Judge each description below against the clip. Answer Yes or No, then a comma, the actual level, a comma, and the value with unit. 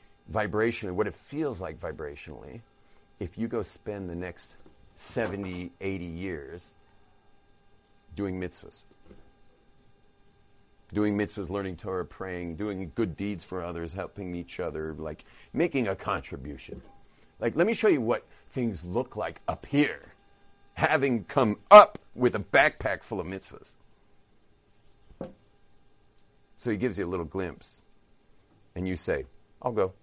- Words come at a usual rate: No, slow, 130 wpm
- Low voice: Yes, low, 100 Hz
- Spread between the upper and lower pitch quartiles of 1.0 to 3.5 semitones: Yes, average, 2.8 semitones